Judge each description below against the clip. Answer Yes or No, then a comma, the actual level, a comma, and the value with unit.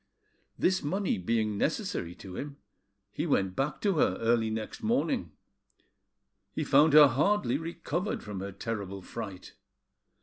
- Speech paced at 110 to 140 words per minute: Yes, slow, 135 wpm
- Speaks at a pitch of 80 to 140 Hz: Yes, low, 135 Hz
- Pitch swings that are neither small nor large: No, wide, 7.8 semitones